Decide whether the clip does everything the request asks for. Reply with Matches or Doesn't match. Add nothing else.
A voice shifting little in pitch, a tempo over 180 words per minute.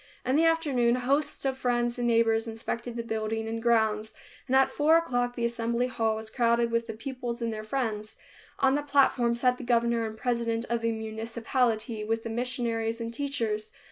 Matches